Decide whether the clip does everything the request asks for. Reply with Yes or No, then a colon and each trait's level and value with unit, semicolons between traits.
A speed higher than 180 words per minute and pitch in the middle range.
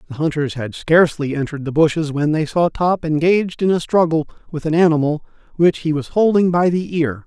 Yes: fast, 205 wpm; medium, 160 Hz